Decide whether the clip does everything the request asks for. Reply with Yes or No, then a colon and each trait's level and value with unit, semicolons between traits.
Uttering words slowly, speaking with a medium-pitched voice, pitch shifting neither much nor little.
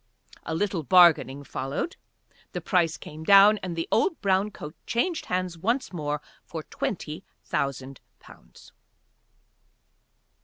Yes: slow, 120 wpm; medium, 175 Hz; average, 4.8 semitones